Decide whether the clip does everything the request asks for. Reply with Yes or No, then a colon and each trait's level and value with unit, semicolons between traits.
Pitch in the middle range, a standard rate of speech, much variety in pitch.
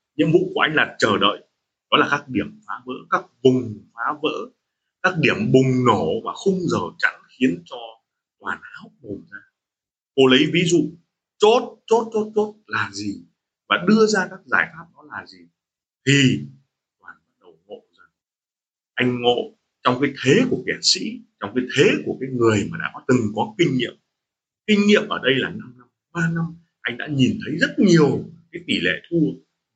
Yes: medium, 150 Hz; average, 190 wpm; wide, 7.6 semitones